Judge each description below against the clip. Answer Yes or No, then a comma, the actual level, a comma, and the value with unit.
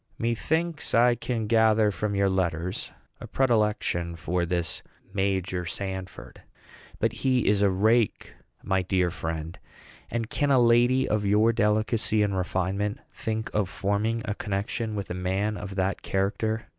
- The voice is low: Yes, low, 105 Hz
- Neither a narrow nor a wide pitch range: Yes, average, 3.2 semitones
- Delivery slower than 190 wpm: Yes, average, 145 wpm